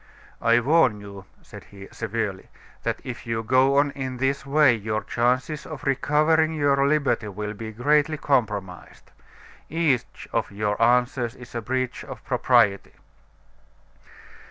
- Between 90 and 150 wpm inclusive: Yes, slow, 135 wpm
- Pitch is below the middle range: Yes, low, 125 Hz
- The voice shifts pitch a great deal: No, average, 4.3 semitones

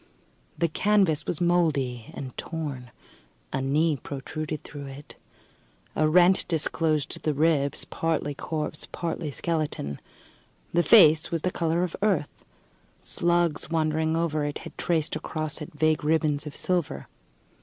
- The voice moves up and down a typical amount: No, narrow, 2.3 semitones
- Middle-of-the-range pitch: Yes, medium, 155 Hz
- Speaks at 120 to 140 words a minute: Yes, slow, 135 wpm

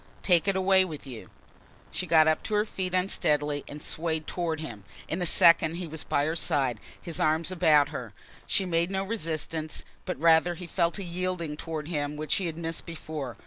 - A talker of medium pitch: Yes, medium, 165 Hz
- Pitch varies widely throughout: No, average, 2.8 semitones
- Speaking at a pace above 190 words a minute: Yes, average, 200 wpm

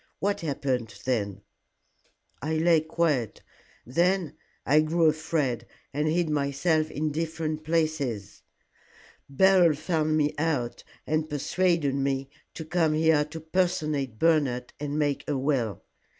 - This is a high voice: No, medium, 155 Hz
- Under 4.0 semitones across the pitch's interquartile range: Yes, average, 2.9 semitones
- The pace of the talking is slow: Yes, slow, 120 wpm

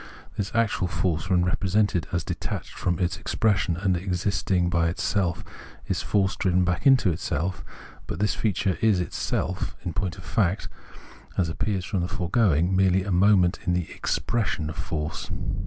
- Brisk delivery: No, average, 160 wpm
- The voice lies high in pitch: No, very low, 90 Hz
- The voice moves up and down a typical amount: No, narrow, 2.1 semitones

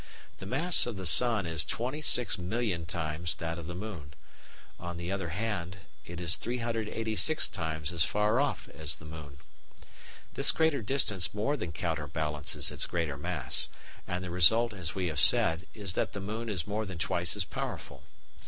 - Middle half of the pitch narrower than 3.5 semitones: No, average, 5.1 semitones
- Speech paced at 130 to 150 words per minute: No, average, 170 wpm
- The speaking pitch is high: No, very low, 90 Hz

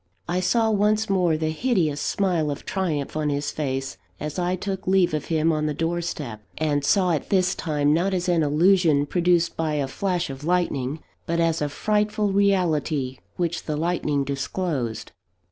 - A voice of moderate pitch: Yes, medium, 165 Hz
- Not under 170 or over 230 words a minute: Yes, average, 175 wpm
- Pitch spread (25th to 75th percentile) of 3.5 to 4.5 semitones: Yes, average, 3.8 semitones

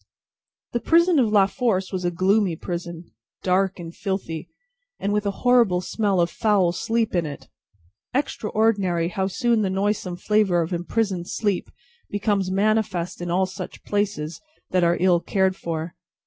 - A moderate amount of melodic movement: Yes, average, 3.1 semitones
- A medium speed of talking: Yes, average, 155 wpm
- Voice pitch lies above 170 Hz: Yes, high, 190 Hz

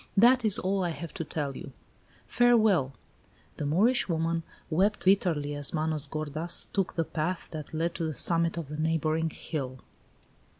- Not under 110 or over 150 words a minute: No, average, 165 wpm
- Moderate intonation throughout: Yes, average, 3.2 semitones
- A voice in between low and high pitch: Yes, medium, 165 Hz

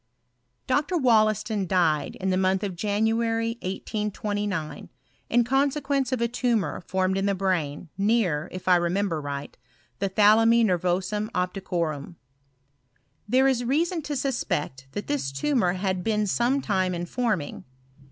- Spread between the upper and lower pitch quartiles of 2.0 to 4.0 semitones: No, average, 4.5 semitones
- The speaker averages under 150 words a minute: Yes, average, 140 wpm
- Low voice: No, high, 205 Hz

